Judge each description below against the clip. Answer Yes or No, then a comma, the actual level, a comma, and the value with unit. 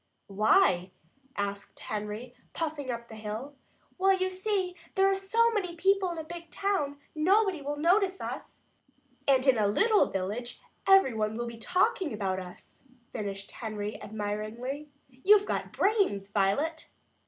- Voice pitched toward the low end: No, very high, 280 Hz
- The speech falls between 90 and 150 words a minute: Yes, average, 145 wpm